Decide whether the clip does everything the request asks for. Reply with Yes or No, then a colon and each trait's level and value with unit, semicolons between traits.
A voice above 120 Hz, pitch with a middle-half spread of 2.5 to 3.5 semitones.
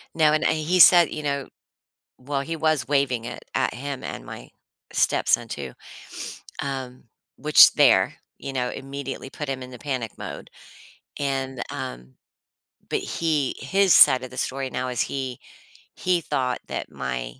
Yes: low, 135 Hz; average, 2.8 semitones